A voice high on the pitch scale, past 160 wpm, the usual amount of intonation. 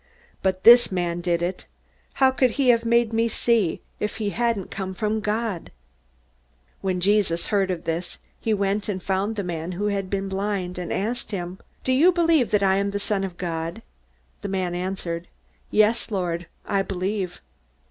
Yes: high, 195 Hz; average, 180 wpm; average, 3.2 semitones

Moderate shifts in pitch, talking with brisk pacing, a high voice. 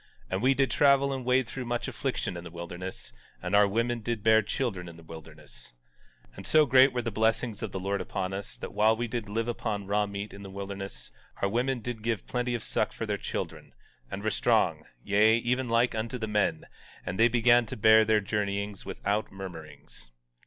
No: average, 3.5 semitones; fast, 210 wpm; low, 110 Hz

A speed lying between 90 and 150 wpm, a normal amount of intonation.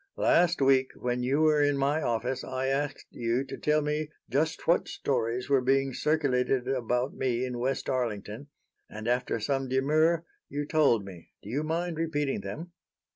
No: average, 170 wpm; average, 3.3 semitones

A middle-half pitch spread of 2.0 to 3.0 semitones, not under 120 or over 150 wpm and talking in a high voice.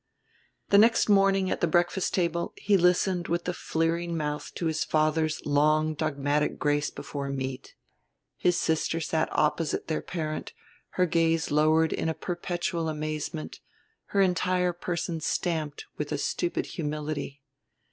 No: narrow, 2.5 semitones; average, 140 wpm; medium, 160 Hz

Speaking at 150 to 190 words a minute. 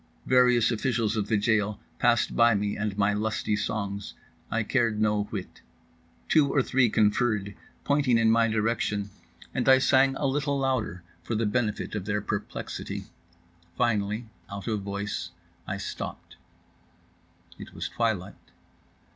No: average, 140 wpm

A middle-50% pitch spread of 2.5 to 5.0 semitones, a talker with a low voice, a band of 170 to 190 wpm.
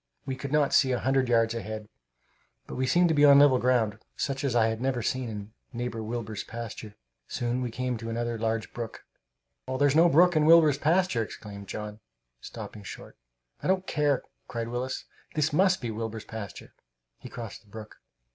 Yes: average, 4.0 semitones; low, 120 Hz; average, 185 wpm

